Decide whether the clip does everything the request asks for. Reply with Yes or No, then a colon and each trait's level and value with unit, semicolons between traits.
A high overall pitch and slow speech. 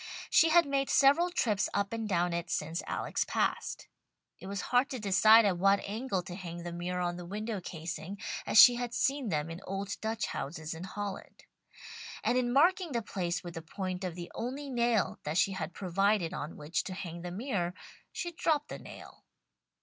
No: high, 195 Hz; average, 195 wpm